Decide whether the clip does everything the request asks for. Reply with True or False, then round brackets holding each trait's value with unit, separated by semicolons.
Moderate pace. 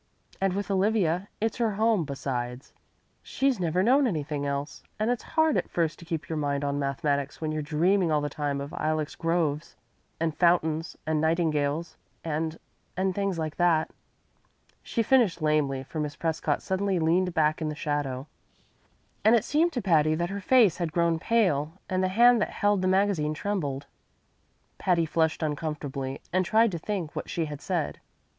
True (175 wpm)